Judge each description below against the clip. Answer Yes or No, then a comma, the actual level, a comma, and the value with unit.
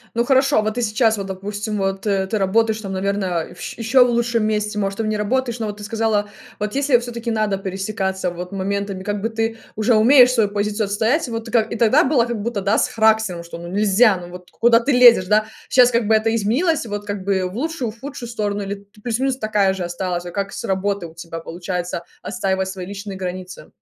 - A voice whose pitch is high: Yes, high, 210 Hz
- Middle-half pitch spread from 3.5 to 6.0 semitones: No, average, 3.0 semitones